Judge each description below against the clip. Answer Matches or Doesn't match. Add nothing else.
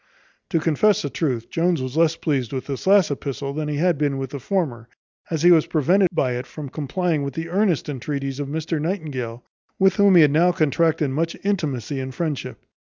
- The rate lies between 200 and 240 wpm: Matches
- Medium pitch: Matches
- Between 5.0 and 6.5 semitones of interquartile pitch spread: Doesn't match